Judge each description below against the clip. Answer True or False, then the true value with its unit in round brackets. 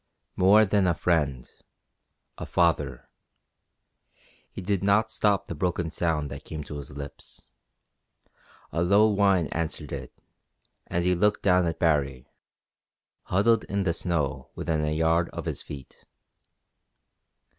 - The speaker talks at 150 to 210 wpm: False (135 wpm)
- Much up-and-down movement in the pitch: False (4.4 semitones)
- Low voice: True (85 Hz)